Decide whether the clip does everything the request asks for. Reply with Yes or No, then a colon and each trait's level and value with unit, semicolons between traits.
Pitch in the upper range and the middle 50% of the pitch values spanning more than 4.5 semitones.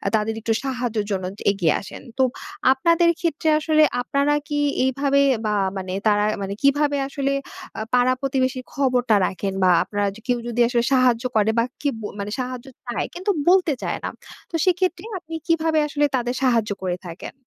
Yes: very high, 255 Hz; average, 4.9 semitones